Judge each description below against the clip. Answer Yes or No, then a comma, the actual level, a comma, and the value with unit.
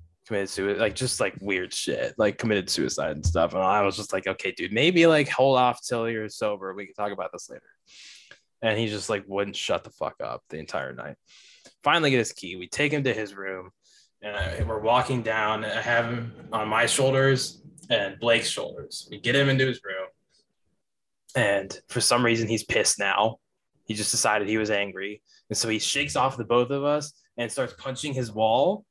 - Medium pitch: No, low, 115 Hz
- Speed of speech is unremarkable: No, fast, 210 wpm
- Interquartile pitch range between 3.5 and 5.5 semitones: Yes, average, 3.9 semitones